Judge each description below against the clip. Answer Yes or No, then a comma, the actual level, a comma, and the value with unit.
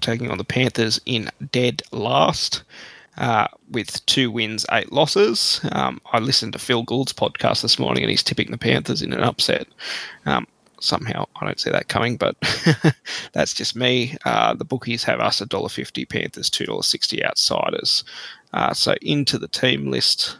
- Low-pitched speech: Yes, low, 125 Hz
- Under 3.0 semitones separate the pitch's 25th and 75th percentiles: Yes, narrow, 2.4 semitones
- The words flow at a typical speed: Yes, average, 175 wpm